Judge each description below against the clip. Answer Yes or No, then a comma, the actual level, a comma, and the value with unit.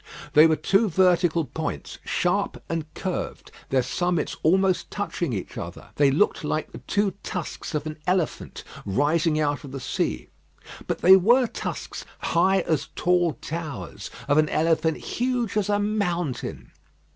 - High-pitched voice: No, medium, 165 Hz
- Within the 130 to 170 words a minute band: Yes, average, 150 wpm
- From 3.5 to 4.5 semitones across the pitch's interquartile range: Yes, average, 3.9 semitones